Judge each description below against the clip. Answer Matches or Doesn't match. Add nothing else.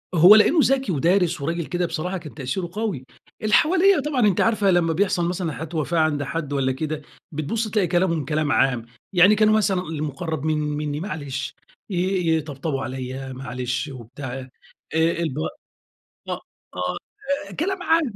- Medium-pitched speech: Matches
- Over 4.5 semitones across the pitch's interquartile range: Matches